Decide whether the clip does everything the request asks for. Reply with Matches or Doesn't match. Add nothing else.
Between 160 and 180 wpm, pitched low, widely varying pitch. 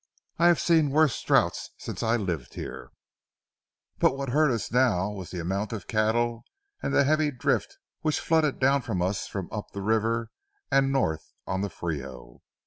Matches